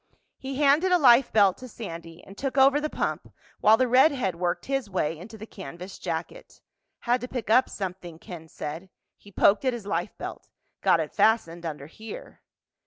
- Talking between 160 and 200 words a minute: Yes, average, 185 wpm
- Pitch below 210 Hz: No, high, 215 Hz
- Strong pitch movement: Yes, wide, 6.8 semitones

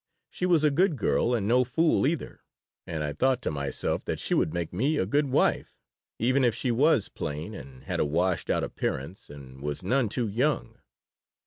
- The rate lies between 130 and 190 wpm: No, average, 200 wpm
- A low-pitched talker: Yes, low, 115 Hz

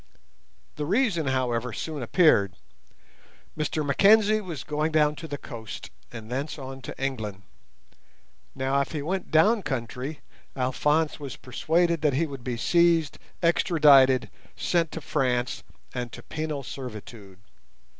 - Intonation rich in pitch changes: No, average, 4.2 semitones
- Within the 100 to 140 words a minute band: Yes, slow, 135 wpm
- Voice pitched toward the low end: No, medium, 145 Hz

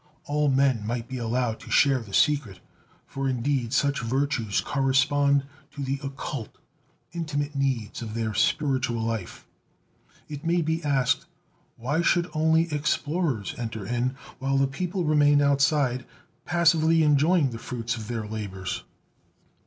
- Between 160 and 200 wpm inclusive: No, slow, 135 wpm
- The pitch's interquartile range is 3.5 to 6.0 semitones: Yes, average, 3.9 semitones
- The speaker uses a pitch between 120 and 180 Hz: Yes, low, 135 Hz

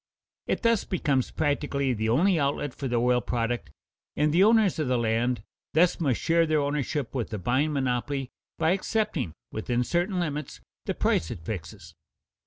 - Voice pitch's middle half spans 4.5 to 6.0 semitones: Yes, average, 5.0 semitones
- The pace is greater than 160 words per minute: Yes, average, 170 wpm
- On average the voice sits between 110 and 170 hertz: Yes, medium, 140 Hz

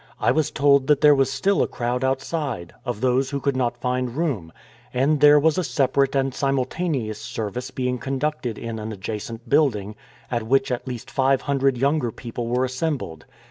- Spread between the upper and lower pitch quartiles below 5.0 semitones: Yes, average, 2.8 semitones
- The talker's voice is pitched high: No, low, 130 Hz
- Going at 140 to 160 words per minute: No, average, 185 wpm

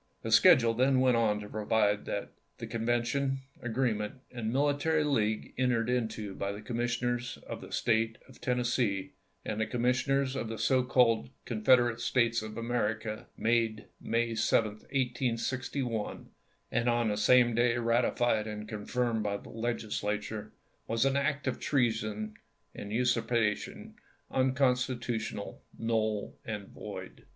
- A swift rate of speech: No, average, 140 wpm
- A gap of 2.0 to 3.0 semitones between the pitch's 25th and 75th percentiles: Yes, narrow, 2.4 semitones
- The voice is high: No, low, 115 Hz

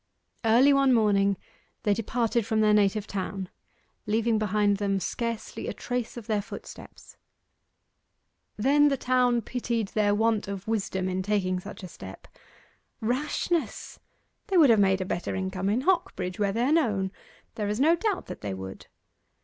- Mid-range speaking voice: No, high, 215 Hz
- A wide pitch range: No, average, 3.8 semitones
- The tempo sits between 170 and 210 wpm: No, average, 160 wpm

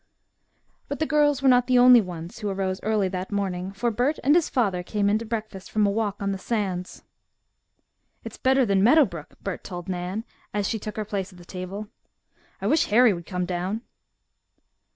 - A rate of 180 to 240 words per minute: Yes, average, 200 wpm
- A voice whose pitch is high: Yes, high, 205 Hz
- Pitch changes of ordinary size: Yes, average, 4.2 semitones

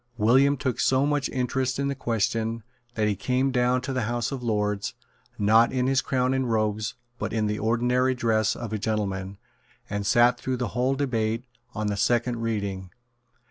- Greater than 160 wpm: Yes, average, 180 wpm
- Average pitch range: Yes, average, 3.1 semitones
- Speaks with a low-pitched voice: Yes, low, 120 Hz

